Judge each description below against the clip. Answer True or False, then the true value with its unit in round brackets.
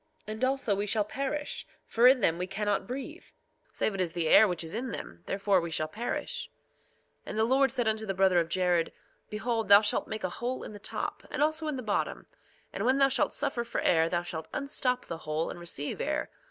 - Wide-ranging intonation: True (6.1 semitones)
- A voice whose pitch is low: False (215 Hz)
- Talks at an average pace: False (230 wpm)